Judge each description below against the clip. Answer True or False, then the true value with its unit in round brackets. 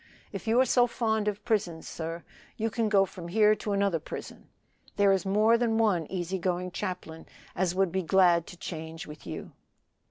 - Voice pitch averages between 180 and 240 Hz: True (190 Hz)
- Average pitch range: True (3.8 semitones)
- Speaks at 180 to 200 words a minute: True (190 wpm)